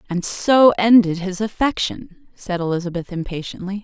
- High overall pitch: Yes, high, 195 Hz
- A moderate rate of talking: No, slow, 125 wpm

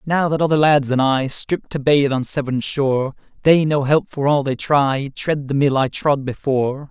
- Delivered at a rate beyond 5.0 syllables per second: No, 4.7 syllables/s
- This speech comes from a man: Yes, male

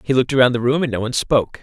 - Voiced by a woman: No, male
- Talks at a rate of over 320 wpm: Yes, fast, 330 wpm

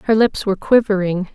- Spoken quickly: No, average, 180 wpm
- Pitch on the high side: Yes, high, 205 Hz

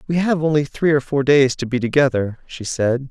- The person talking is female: No, male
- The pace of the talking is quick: Yes, fast, 230 wpm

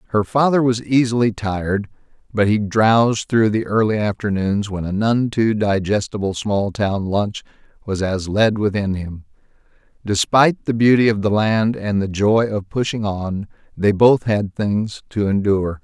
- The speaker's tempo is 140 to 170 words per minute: Yes, average, 165 wpm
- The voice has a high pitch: No, low, 105 Hz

